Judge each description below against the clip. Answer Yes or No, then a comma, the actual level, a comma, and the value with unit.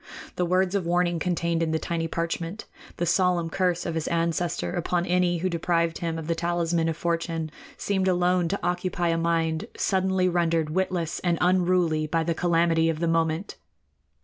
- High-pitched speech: No, medium, 170 Hz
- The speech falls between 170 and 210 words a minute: Yes, average, 175 wpm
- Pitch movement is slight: Yes, narrow, 1.4 semitones